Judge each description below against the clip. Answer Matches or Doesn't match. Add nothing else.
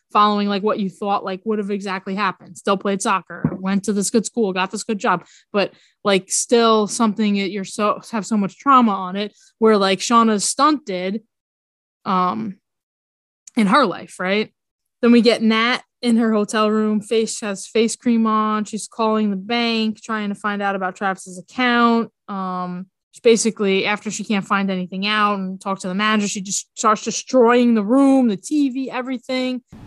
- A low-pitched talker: Doesn't match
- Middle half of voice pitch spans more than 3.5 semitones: Doesn't match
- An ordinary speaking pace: Matches